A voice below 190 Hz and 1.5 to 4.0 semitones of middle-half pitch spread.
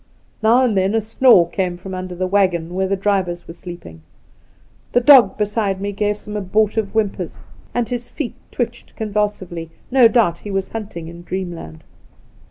No: high, 200 Hz; average, 3.6 semitones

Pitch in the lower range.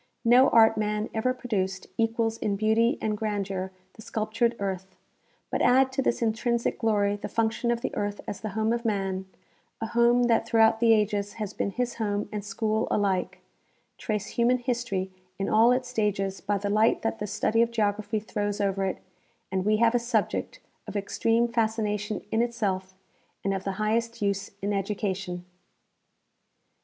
No: high, 215 Hz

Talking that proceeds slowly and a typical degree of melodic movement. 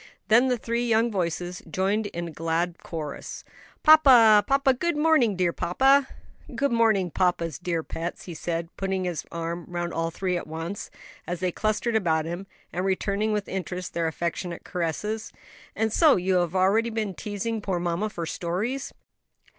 No: average, 165 wpm; average, 4.5 semitones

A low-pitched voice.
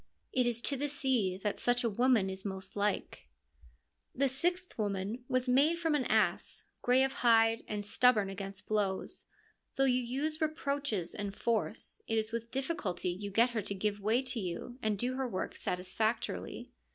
No: high, 230 Hz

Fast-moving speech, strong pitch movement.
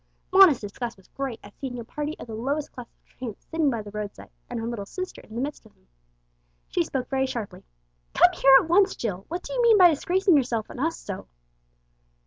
Yes: fast, 225 wpm; wide, 6.3 semitones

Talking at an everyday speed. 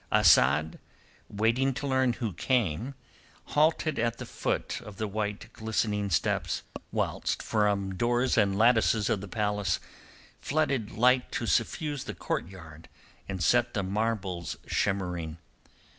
No: slow, 130 wpm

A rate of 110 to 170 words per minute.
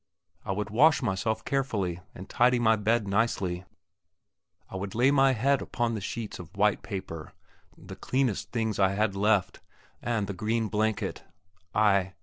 Yes: average, 155 wpm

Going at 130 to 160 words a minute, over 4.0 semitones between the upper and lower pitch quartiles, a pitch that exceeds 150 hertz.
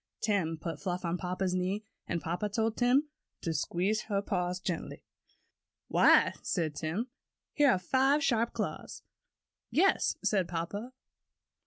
Yes: slow, 135 wpm; average, 4.6 semitones; high, 190 Hz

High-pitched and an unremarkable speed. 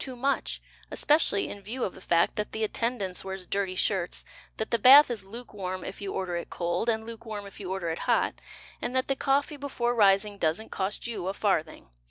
No: high, 205 Hz; fast, 210 wpm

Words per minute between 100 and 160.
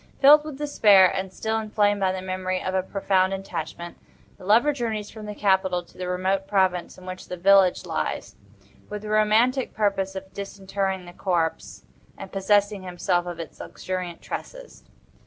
No: average, 170 wpm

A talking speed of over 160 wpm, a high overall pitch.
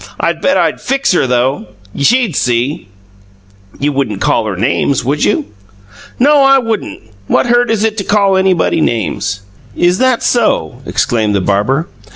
No: average, 170 wpm; medium, 145 Hz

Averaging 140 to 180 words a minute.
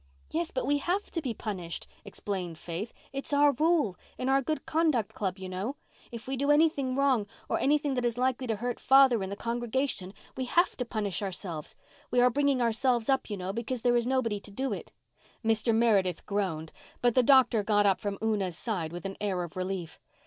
No: average, 200 wpm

